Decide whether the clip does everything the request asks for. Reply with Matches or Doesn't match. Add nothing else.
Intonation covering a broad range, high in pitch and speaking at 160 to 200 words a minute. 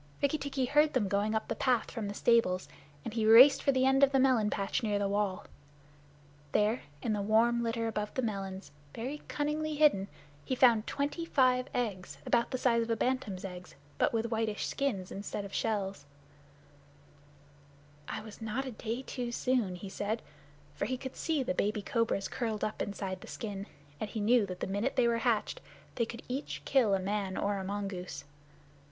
Doesn't match